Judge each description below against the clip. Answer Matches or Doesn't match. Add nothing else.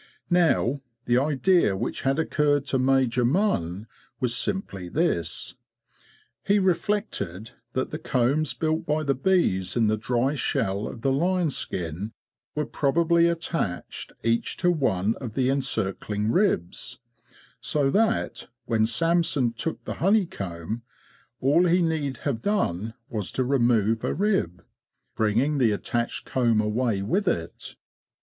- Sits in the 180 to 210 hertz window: Doesn't match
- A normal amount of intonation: Doesn't match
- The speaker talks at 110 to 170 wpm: Matches